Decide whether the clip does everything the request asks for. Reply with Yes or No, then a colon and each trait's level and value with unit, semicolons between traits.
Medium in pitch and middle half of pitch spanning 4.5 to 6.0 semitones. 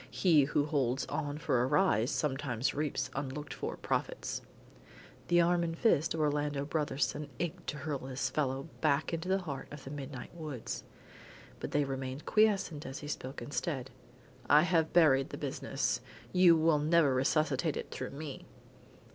No: medium, 145 Hz; average, 3.2 semitones